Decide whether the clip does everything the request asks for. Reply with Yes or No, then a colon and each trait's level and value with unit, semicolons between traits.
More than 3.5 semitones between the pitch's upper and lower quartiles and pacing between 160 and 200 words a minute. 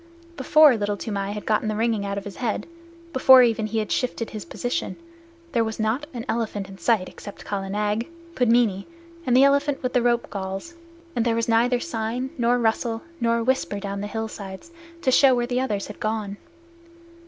No: average, 3.1 semitones; average, 190 wpm